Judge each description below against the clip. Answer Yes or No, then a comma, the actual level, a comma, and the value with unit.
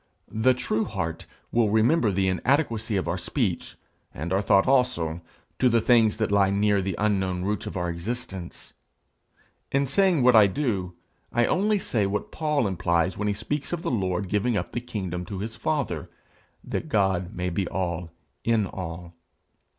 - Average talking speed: Yes, average, 175 wpm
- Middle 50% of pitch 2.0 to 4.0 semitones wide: No, average, 4.7 semitones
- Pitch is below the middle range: Yes, low, 105 Hz